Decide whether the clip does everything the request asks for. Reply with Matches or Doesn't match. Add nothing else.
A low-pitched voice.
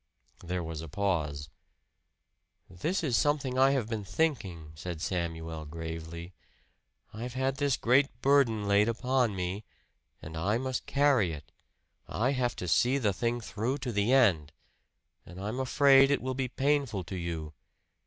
Matches